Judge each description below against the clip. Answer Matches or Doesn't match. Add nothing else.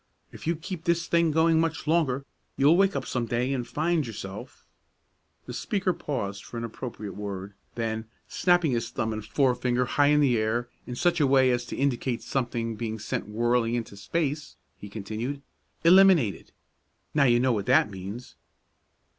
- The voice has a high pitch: Doesn't match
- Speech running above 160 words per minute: Matches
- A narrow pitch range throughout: Doesn't match